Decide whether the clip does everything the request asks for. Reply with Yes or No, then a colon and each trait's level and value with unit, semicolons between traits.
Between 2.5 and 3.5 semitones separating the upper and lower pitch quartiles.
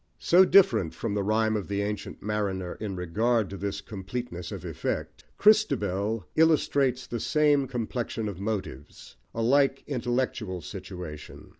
No: average, 4.7 semitones